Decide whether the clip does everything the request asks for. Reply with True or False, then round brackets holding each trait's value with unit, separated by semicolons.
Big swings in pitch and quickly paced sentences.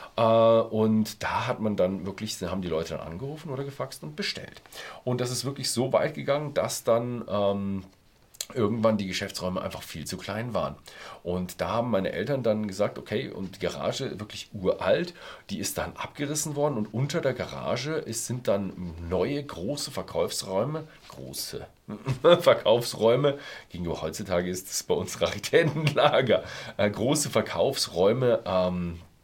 False (6.2 semitones; 155 wpm)